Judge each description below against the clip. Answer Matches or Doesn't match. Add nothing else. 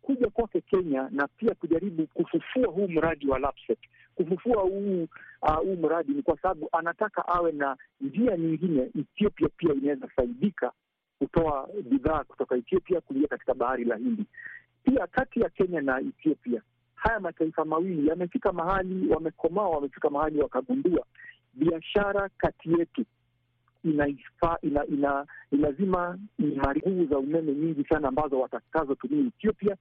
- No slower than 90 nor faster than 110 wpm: Doesn't match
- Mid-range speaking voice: Matches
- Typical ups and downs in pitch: Doesn't match